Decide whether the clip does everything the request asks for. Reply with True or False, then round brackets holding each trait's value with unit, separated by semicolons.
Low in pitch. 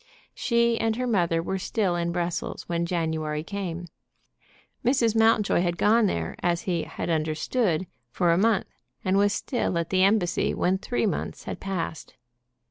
False (185 Hz)